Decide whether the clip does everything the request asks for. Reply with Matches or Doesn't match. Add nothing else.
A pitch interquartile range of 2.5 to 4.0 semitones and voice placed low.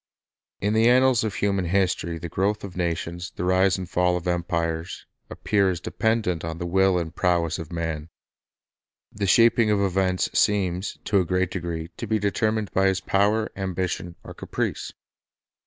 Matches